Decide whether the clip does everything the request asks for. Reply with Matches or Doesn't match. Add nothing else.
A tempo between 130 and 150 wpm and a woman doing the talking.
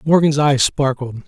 Doesn't match